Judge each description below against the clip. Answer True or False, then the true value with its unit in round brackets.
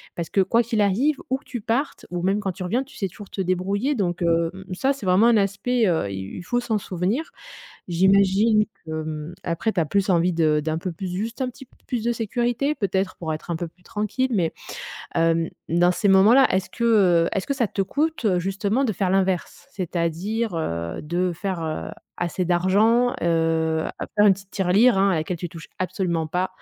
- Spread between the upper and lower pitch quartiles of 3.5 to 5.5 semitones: True (4.6 semitones)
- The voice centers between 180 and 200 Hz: True (190 Hz)